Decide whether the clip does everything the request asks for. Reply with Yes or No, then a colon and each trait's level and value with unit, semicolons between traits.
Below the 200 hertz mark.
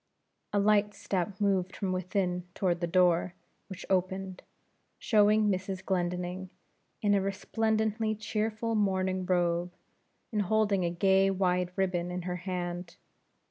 Yes: high, 190 Hz